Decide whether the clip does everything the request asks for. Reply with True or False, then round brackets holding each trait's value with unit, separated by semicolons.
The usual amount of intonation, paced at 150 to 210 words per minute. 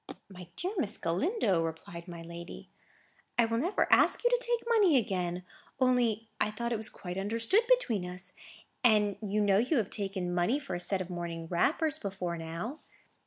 False (6.2 semitones; 175 wpm)